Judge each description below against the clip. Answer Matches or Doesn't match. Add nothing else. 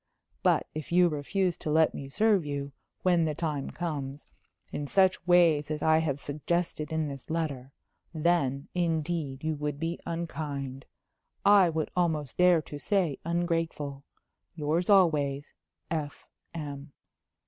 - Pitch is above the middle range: Doesn't match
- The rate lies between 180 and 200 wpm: Doesn't match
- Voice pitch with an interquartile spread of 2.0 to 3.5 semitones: Matches